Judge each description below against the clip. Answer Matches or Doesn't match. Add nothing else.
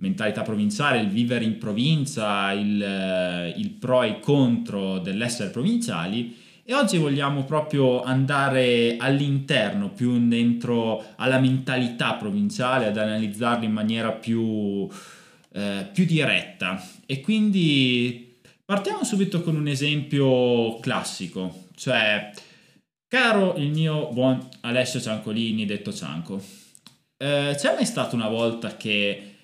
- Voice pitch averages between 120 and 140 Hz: Matches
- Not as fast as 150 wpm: Matches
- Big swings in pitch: Doesn't match